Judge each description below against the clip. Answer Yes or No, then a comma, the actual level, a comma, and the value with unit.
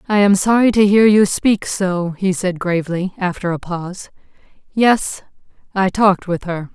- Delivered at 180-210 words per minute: No, average, 170 wpm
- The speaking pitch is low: No, high, 190 Hz